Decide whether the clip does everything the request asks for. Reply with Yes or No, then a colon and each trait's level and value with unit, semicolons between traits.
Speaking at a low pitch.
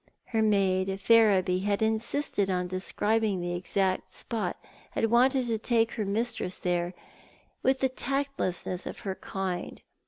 No: high, 205 Hz